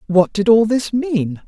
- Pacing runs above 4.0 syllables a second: No, 3.9 syllables/s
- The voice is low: No, high, 215 Hz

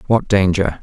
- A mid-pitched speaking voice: No, low, 100 Hz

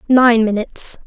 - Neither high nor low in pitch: No, high, 235 Hz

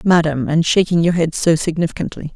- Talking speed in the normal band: Yes, average, 180 wpm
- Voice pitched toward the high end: No, medium, 165 Hz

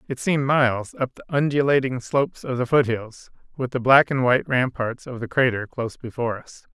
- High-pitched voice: No, low, 125 Hz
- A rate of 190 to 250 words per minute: Yes, average, 195 wpm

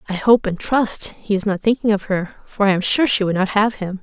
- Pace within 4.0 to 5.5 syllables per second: Yes, 5.4 syllables/s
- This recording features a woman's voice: Yes, female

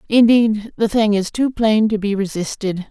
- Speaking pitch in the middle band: No, high, 215 Hz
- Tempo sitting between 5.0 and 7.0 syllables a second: No, 4.6 syllables/s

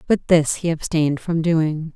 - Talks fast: No, average, 185 wpm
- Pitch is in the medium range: Yes, medium, 160 Hz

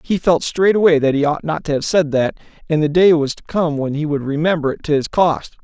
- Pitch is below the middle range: No, medium, 155 Hz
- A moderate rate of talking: No, fast, 265 wpm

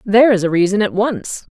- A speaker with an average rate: No, fast, 230 wpm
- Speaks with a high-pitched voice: Yes, high, 210 Hz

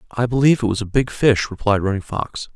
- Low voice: Yes, low, 115 Hz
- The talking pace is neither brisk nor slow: No, fast, 235 wpm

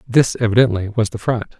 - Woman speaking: No, male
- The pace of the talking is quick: No, average, 190 wpm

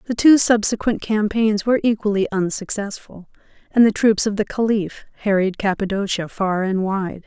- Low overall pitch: No, high, 205 Hz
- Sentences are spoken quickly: No, average, 150 wpm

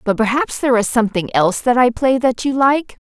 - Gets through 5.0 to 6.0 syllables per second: Yes, 5.9 syllables/s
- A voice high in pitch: Yes, high, 245 Hz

